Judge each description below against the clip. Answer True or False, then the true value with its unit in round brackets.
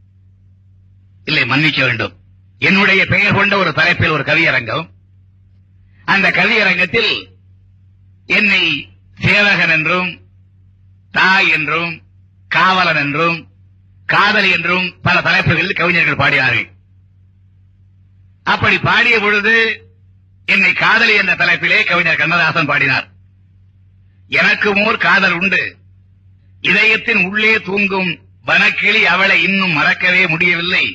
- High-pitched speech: False (135 Hz)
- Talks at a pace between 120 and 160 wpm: False (90 wpm)